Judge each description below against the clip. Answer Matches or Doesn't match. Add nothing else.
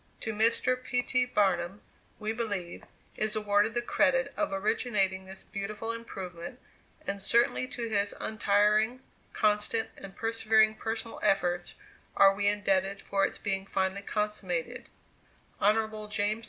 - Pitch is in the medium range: Doesn't match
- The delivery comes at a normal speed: Doesn't match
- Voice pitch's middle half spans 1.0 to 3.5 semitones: Matches